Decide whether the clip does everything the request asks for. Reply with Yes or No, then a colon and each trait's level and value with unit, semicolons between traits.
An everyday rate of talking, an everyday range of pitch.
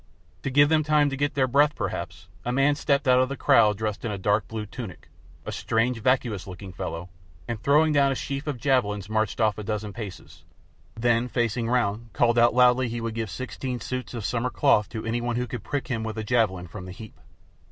No: fast, 225 wpm; average, 3.3 semitones